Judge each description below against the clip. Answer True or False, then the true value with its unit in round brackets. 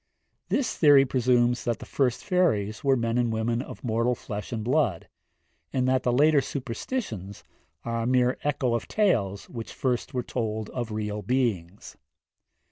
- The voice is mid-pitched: False (120 Hz)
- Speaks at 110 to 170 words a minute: True (160 wpm)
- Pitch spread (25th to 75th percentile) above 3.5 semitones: False (3.1 semitones)